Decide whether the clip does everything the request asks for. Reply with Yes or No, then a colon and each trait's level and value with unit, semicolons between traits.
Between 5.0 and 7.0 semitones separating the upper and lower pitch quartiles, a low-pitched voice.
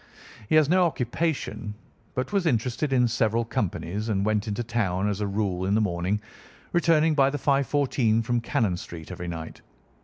Yes: average, 5.3 semitones; low, 115 Hz